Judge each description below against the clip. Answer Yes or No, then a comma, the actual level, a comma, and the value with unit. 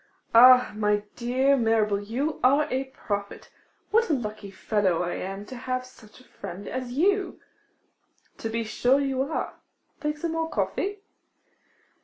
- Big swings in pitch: No, average, 4.8 semitones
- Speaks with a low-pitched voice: No, very high, 250 Hz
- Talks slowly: No, average, 150 wpm